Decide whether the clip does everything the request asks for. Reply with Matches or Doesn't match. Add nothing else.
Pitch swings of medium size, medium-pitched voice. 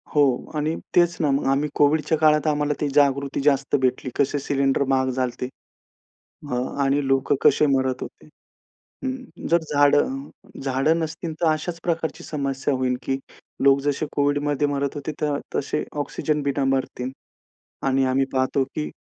Doesn't match